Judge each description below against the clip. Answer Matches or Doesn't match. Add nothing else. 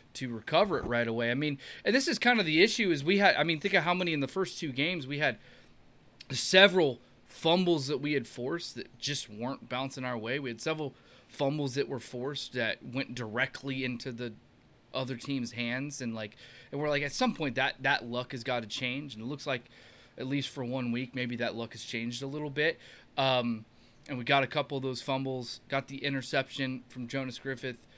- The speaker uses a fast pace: Matches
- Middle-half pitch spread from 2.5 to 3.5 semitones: Matches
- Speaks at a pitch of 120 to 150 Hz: Matches